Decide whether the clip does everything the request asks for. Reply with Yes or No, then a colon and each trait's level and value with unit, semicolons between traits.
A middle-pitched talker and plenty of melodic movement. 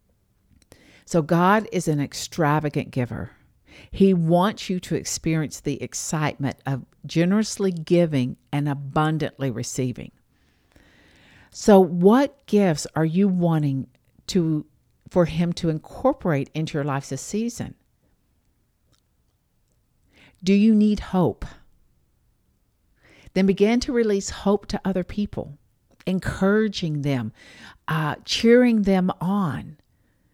Yes: medium, 160 Hz; wide, 6.2 semitones